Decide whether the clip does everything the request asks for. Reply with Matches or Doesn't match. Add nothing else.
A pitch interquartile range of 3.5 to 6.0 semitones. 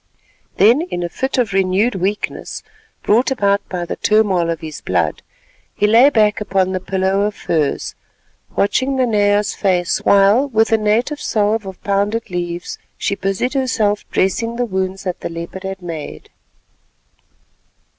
Doesn't match